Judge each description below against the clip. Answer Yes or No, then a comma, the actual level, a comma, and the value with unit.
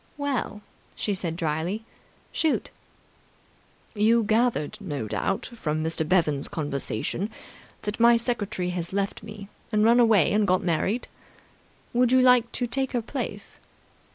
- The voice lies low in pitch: No, high, 210 Hz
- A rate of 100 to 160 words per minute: Yes, slow, 135 wpm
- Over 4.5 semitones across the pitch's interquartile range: Yes, wide, 5.4 semitones